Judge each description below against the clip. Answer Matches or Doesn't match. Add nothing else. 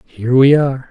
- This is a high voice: Doesn't match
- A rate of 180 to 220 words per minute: Matches